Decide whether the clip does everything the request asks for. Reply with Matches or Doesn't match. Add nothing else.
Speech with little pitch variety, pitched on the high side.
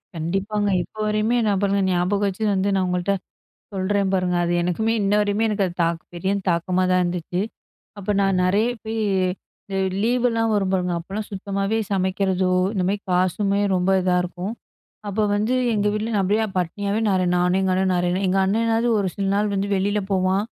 Matches